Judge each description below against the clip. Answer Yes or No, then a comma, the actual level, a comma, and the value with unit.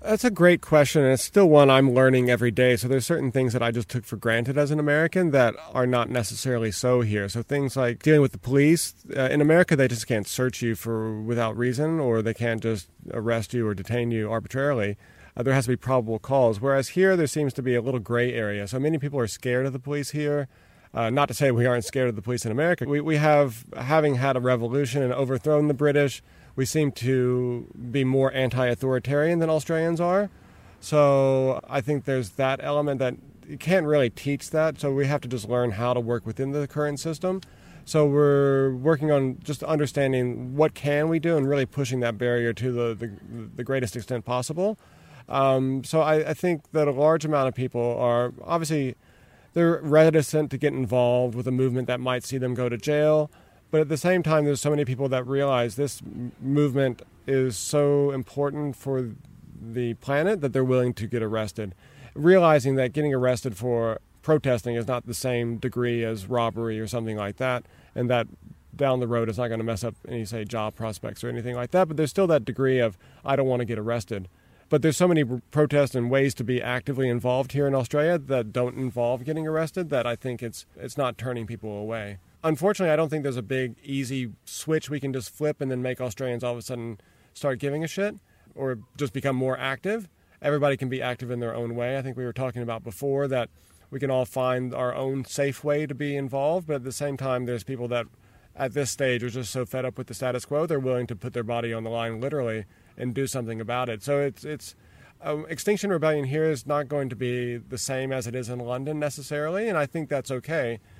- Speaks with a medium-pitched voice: No, low, 130 Hz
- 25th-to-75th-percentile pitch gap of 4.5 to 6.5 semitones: No, average, 3.3 semitones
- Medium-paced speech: No, fast, 220 wpm